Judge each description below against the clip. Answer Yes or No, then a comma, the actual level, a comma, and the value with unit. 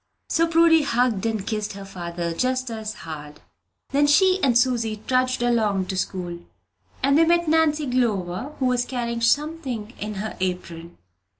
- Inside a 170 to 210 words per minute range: No, average, 160 wpm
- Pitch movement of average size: No, wide, 6.2 semitones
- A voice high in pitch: Yes, high, 235 Hz